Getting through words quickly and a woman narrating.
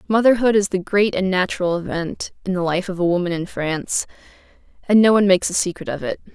Yes: fast, 215 wpm; female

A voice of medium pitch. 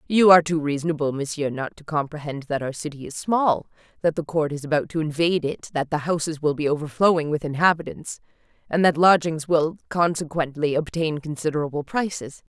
Yes: medium, 155 Hz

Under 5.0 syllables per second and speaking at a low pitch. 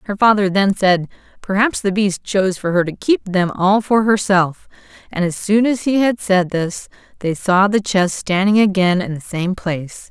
No: 4.6 syllables/s; high, 195 Hz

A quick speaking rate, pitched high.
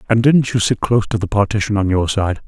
No: fast, 265 wpm; low, 105 Hz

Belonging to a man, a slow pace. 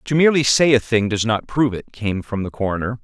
No: male; fast, 255 wpm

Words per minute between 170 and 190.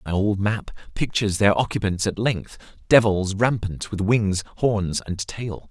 No: average, 145 wpm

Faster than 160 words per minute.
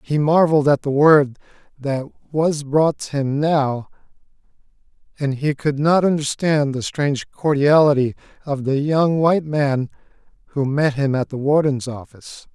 No: average, 150 wpm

